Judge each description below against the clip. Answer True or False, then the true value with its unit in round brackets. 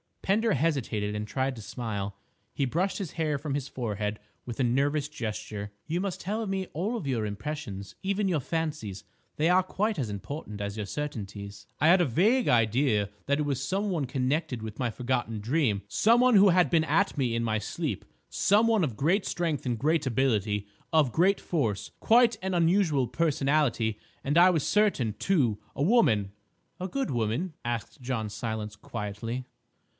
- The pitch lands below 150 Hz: True (140 Hz)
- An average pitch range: False (7.9 semitones)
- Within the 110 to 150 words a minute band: False (170 wpm)